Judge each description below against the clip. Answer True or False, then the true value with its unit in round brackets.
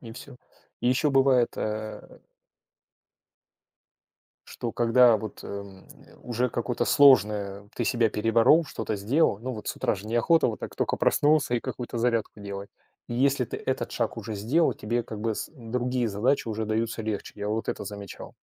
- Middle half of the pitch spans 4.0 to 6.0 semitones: False (2.9 semitones)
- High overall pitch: False (115 Hz)